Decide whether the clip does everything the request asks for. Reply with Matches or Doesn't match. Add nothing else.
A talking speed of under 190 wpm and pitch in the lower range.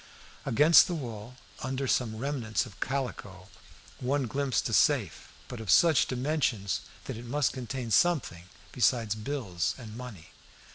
Matches